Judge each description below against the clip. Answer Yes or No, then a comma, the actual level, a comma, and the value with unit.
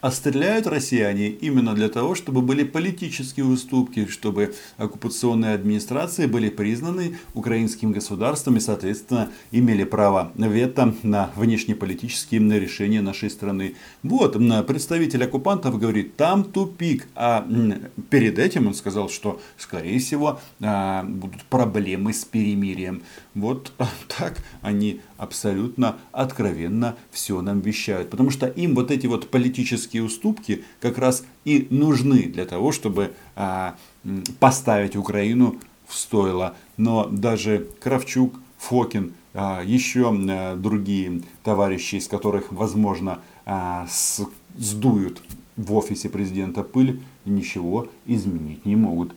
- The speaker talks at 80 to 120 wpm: Yes, average, 115 wpm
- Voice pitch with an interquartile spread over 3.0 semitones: Yes, average, 4.2 semitones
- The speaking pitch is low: Yes, low, 110 Hz